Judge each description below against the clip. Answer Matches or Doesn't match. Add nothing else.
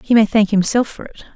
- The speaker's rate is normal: Doesn't match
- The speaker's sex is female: Matches